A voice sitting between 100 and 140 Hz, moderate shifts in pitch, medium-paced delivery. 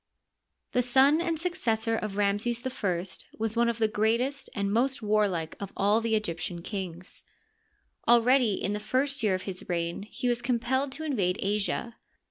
No: high, 225 Hz; average, 3.9 semitones; average, 175 wpm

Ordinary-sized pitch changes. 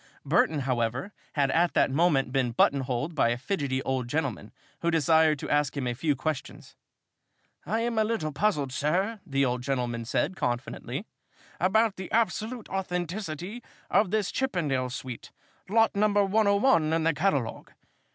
No: wide, 7.0 semitones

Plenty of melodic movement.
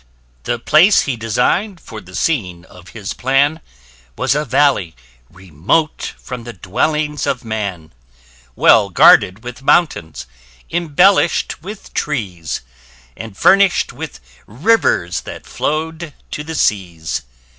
Yes: wide, 8.6 semitones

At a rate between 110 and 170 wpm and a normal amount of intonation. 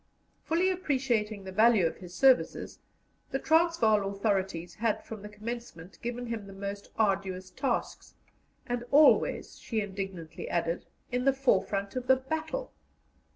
Yes: average, 140 wpm; average, 5.0 semitones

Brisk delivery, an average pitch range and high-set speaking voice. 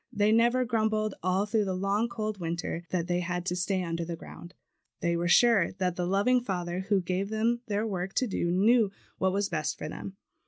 Yes: fast, 210 wpm; average, 3.5 semitones; high, 195 Hz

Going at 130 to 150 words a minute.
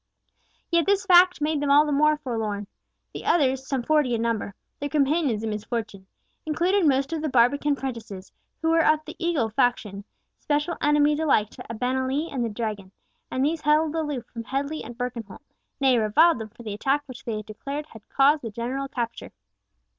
No: average, 185 wpm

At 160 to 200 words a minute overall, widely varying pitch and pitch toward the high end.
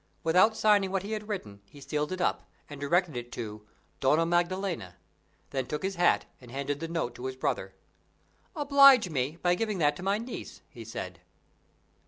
No: average, 185 wpm; wide, 6.2 semitones; medium, 170 Hz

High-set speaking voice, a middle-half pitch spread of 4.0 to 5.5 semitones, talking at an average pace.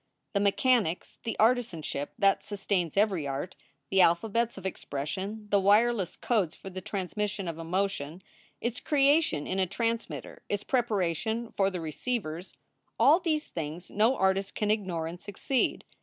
Yes: high, 195 Hz; average, 4.6 semitones; average, 150 wpm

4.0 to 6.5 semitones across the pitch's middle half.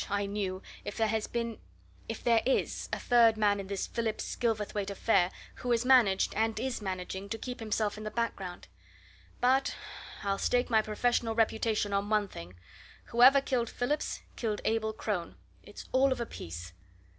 No: average, 2.9 semitones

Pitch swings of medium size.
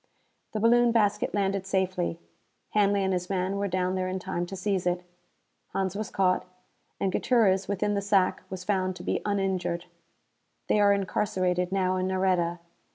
No: narrow, 1.6 semitones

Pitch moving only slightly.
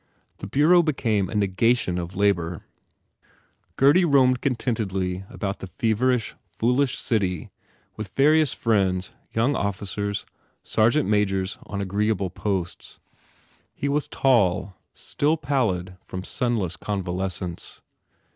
No: average, 5.3 semitones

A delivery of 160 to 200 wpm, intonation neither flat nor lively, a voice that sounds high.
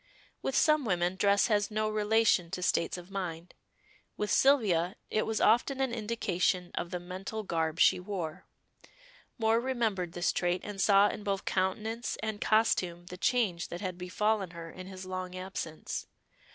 Yes: average, 165 wpm; average, 3.5 semitones; high, 195 Hz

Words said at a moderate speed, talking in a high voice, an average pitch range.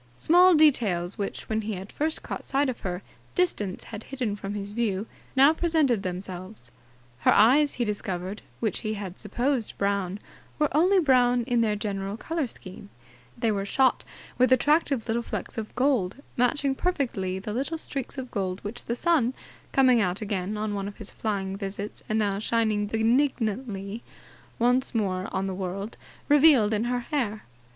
Yes: average, 170 wpm; high, 220 Hz; average, 4.7 semitones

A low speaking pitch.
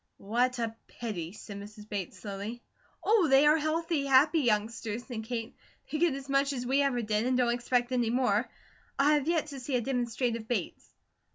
No: high, 245 Hz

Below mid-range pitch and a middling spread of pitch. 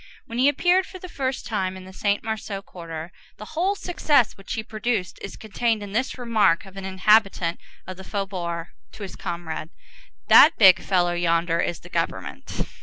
No: high, 195 Hz; average, 4.7 semitones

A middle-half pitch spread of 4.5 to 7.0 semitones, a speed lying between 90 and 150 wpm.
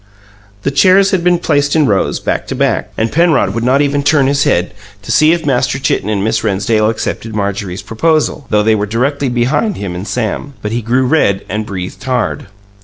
No: average, 5.3 semitones; fast, 205 wpm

